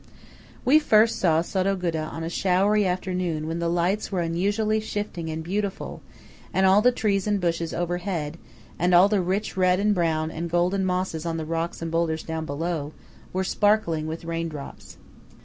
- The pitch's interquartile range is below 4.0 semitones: Yes, average, 3.1 semitones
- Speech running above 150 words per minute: Yes, average, 175 wpm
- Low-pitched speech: No, medium, 175 Hz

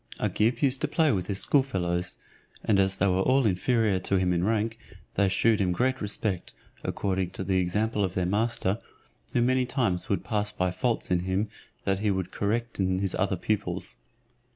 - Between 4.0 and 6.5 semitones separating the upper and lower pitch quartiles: No, average, 3.5 semitones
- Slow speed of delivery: No, average, 190 wpm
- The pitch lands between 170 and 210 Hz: No, low, 100 Hz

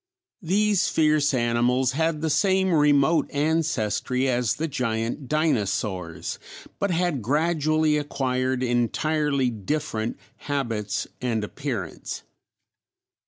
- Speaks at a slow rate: Yes, slow, 95 wpm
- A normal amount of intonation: Yes, average, 4.7 semitones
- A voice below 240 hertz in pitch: Yes, medium, 140 Hz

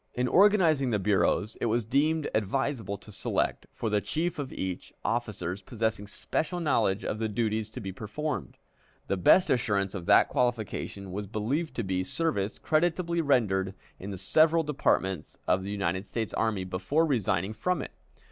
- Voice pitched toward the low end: Yes, low, 110 Hz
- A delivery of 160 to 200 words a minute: Yes, average, 165 wpm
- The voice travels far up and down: Yes, wide, 6.8 semitones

